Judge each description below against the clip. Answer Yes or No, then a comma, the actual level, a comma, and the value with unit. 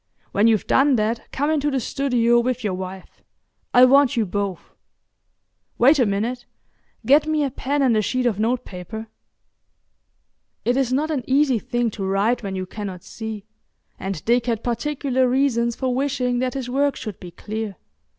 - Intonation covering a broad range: No, average, 3.9 semitones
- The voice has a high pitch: Yes, high, 240 Hz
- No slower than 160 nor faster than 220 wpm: Yes, average, 170 wpm